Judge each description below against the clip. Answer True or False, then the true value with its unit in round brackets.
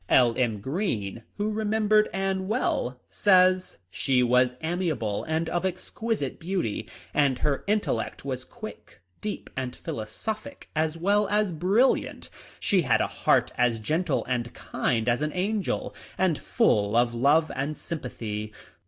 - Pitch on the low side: False (155 Hz)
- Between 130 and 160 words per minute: True (145 wpm)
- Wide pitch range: True (7.7 semitones)